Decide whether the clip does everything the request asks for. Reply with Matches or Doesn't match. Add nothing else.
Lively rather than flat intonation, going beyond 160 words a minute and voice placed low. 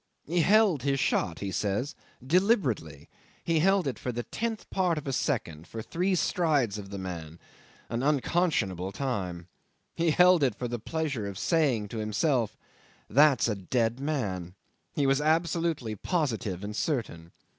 Doesn't match